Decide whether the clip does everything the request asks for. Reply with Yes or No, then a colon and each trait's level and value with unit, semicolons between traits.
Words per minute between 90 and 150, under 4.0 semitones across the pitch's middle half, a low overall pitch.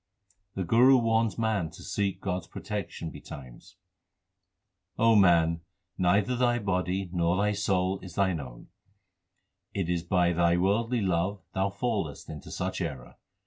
Yes: average, 145 wpm; average, 3.4 semitones; very low, 95 Hz